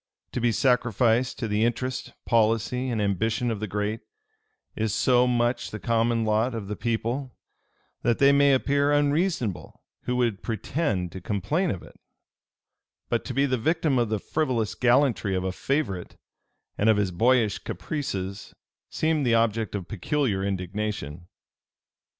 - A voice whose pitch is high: No, low, 115 Hz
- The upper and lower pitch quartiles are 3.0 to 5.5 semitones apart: Yes, average, 3.8 semitones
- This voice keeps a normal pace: Yes, average, 150 wpm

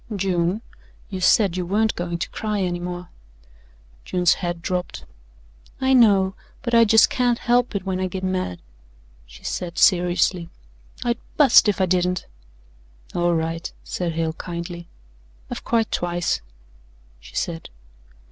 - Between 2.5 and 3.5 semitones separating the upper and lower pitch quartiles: Yes, average, 3.2 semitones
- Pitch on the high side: No, medium, 180 Hz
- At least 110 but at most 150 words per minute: Yes, average, 140 wpm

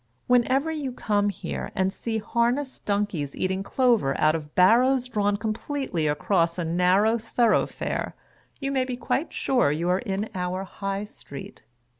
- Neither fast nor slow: Yes, average, 155 wpm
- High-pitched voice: Yes, high, 205 Hz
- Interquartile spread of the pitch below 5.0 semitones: No, average, 5.3 semitones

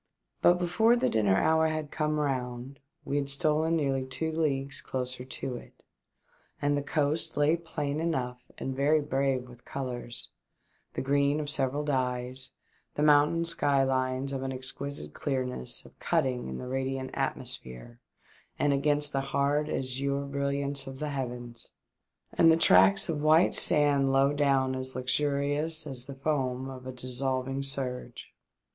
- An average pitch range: No, narrow, 2.2 semitones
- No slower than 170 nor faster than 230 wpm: No, average, 150 wpm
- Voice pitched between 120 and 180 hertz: Yes, medium, 140 Hz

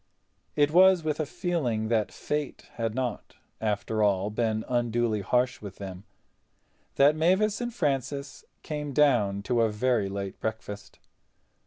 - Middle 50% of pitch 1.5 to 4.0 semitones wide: No, wide, 5.6 semitones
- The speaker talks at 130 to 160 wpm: Yes, average, 140 wpm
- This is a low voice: Yes, low, 120 Hz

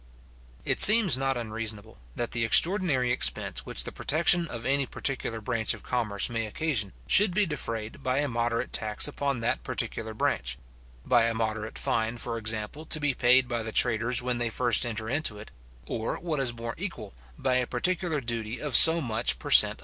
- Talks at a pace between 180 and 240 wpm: Yes, average, 190 wpm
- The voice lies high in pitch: No, low, 120 Hz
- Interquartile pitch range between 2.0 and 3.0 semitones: No, average, 3.9 semitones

